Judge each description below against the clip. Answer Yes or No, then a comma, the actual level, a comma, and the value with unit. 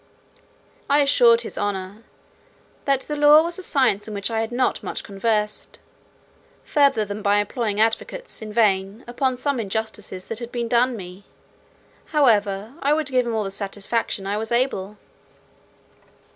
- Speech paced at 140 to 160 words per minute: Yes, average, 155 wpm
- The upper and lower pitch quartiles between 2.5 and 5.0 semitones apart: Yes, average, 4.0 semitones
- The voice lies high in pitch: Yes, high, 225 Hz